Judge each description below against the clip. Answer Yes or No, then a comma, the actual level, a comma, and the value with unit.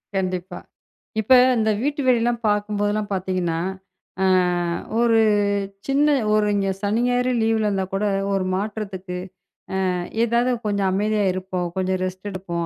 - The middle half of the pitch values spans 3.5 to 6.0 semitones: No, average, 2.9 semitones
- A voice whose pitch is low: No, high, 205 Hz